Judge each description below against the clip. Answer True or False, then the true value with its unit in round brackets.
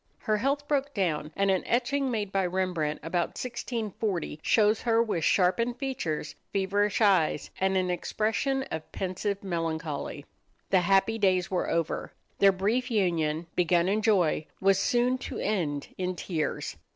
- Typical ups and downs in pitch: True (4.5 semitones)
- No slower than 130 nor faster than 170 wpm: True (150 wpm)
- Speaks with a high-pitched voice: True (195 Hz)